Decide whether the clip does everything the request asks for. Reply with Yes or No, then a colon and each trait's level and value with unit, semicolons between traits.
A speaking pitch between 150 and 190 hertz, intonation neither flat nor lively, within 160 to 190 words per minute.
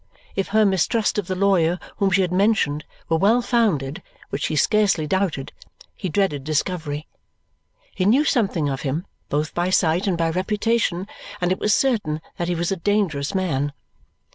Yes: medium, 185 Hz; average, 4.4 semitones; average, 170 wpm